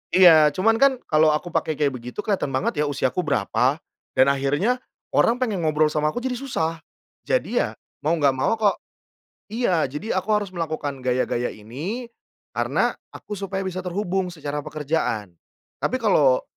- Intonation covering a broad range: Yes, wide, 5.8 semitones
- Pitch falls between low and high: Yes, medium, 160 Hz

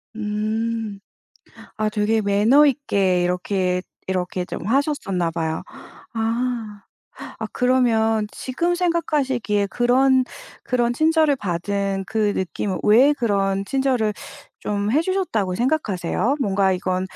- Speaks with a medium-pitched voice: No, high, 220 Hz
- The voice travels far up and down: No, average, 4.8 semitones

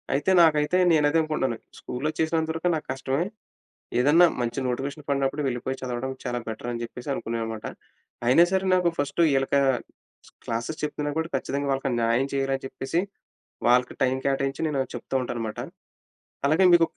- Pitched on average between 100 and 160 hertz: Yes, low, 135 Hz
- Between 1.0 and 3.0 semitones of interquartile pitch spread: No, average, 3.7 semitones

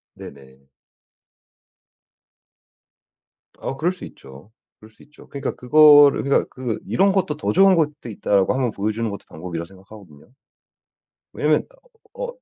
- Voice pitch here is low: Yes, low, 120 Hz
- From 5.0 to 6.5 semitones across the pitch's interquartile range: No, wide, 7.8 semitones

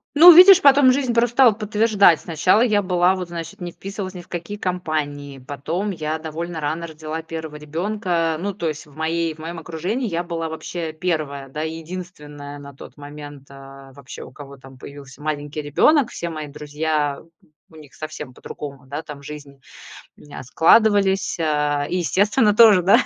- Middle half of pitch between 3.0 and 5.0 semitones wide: Yes, average, 4.2 semitones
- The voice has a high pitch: No, medium, 160 Hz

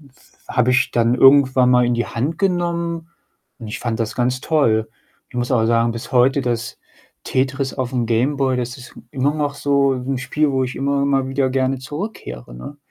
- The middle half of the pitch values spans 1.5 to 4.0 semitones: Yes, narrow, 2.5 semitones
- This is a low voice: Yes, low, 130 Hz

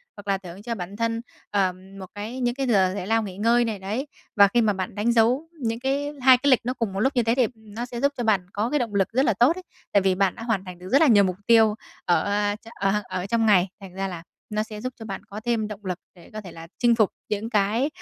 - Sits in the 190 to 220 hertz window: Yes, high, 215 Hz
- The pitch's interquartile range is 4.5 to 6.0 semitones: No, average, 3.4 semitones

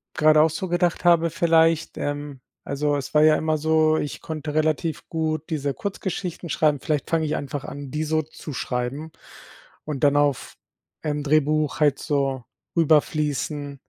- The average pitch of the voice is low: No, medium, 155 Hz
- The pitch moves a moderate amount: No, narrow, 1.7 semitones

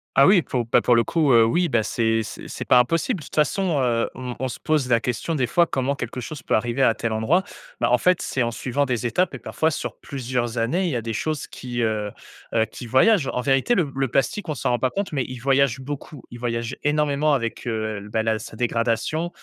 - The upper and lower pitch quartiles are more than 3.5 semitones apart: Yes, average, 4.4 semitones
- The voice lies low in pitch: Yes, low, 125 Hz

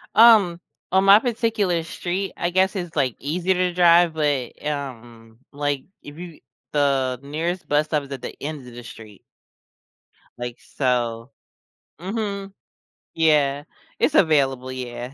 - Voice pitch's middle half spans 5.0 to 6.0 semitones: Yes, wide, 5.6 semitones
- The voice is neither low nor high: Yes, medium, 150 Hz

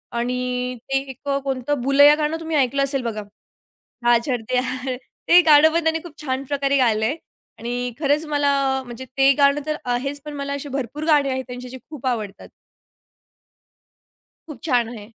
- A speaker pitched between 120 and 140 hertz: No, very high, 270 Hz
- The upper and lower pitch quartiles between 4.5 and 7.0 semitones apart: No, average, 2.8 semitones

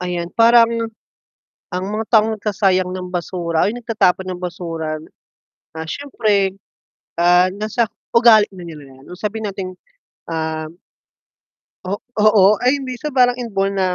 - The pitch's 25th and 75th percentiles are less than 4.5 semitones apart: Yes, average, 4.1 semitones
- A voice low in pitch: No, high, 195 Hz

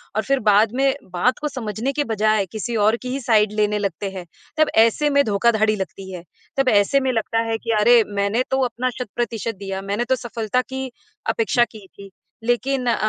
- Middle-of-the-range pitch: No, high, 225 Hz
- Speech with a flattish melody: No, average, 3.4 semitones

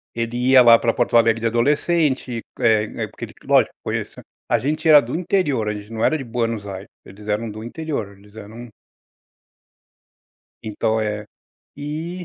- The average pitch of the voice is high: No, low, 115 Hz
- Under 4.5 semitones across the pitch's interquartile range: No, average, 4.8 semitones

